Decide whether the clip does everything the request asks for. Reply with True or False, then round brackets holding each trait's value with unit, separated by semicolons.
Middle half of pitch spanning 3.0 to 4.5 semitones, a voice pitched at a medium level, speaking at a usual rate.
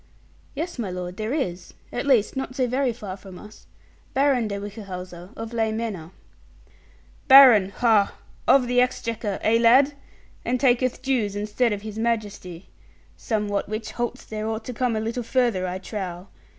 False (3.6 semitones; 220 Hz; 165 wpm)